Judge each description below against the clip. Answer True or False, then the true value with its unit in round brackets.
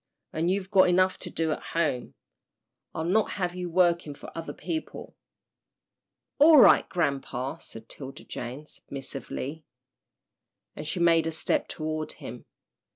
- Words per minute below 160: True (140 wpm)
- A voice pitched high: False (165 Hz)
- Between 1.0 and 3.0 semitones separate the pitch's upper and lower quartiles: False (3.6 semitones)